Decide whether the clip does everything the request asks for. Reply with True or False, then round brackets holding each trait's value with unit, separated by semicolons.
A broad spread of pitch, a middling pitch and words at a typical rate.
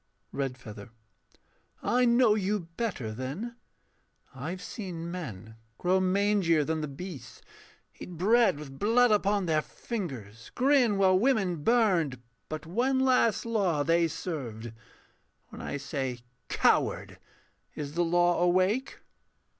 False (6.7 semitones; 175 Hz; 120 wpm)